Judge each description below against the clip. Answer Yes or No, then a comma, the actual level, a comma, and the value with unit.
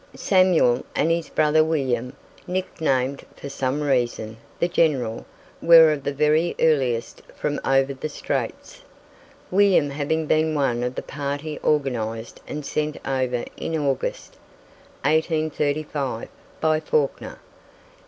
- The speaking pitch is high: No, medium, 145 Hz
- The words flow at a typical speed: No, slow, 120 wpm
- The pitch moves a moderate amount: Yes, average, 3.1 semitones